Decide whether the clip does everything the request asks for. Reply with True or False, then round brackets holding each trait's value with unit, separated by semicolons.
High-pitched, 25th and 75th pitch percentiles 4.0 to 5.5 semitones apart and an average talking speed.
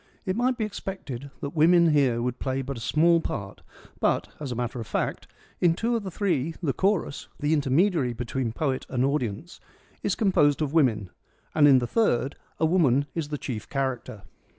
False (145 Hz; 5.1 semitones; 190 wpm)